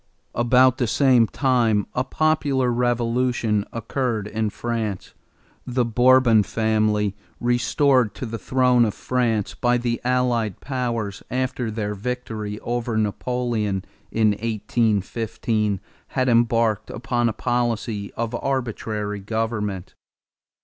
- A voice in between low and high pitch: No, low, 115 Hz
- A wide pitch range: No, narrow, 2.6 semitones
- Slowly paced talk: Yes, slow, 110 wpm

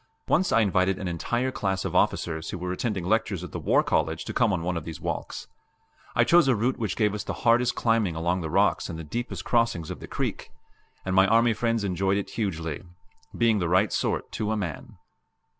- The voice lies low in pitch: Yes, low, 100 Hz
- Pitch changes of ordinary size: Yes, average, 4.5 semitones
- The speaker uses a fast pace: Yes, fast, 220 wpm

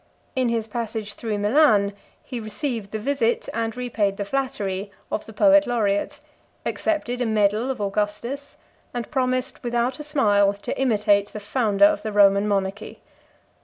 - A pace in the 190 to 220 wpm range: No, average, 155 wpm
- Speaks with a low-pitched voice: No, high, 225 Hz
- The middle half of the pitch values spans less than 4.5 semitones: Yes, average, 3.8 semitones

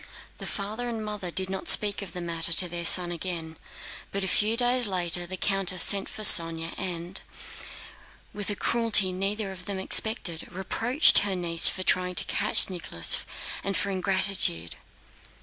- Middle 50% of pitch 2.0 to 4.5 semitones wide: Yes, average, 2.9 semitones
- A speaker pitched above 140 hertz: Yes, high, 190 Hz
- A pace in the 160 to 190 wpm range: Yes, average, 165 wpm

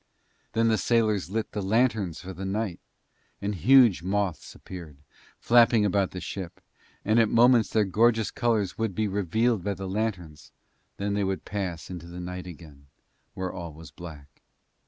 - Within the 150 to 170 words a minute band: Yes, average, 165 wpm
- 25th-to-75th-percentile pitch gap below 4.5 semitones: Yes, average, 3.9 semitones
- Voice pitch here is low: Yes, low, 100 Hz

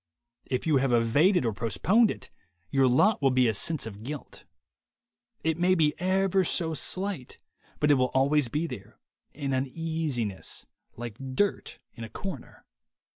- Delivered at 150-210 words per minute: Yes, average, 155 wpm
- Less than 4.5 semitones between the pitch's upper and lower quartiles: No, wide, 5.4 semitones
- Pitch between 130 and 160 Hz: Yes, medium, 140 Hz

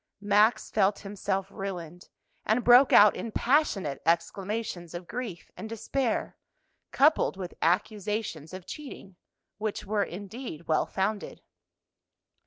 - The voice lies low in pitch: No, high, 205 Hz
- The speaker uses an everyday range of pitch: Yes, average, 3.8 semitones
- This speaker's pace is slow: Yes, slow, 115 wpm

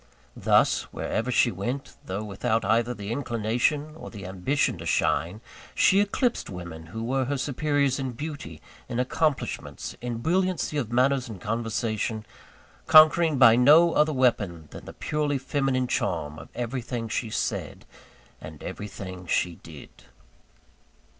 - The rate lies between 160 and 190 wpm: No, average, 140 wpm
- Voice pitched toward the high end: No, low, 120 Hz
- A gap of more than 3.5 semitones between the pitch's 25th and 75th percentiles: Yes, average, 5.2 semitones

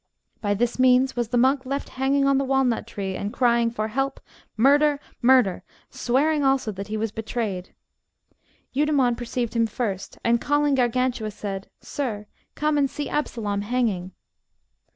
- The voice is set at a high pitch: Yes, high, 245 Hz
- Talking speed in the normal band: Yes, average, 150 wpm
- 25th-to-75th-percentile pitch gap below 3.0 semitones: No, average, 3.9 semitones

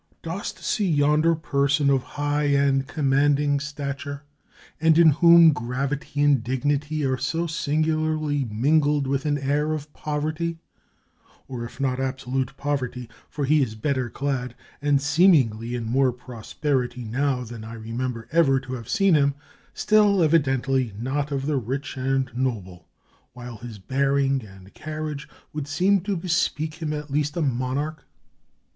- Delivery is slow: No, average, 155 wpm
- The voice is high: No, medium, 140 Hz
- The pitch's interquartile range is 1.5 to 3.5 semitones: Yes, average, 2.9 semitones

